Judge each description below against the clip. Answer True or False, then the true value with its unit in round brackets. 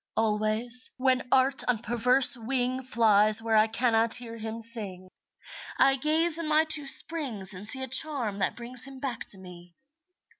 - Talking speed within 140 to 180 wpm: True (165 wpm)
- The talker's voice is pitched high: True (240 Hz)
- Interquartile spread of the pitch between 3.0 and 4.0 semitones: True (3.4 semitones)